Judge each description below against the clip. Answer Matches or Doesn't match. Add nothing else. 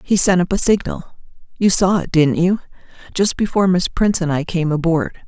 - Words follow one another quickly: Doesn't match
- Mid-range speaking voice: Matches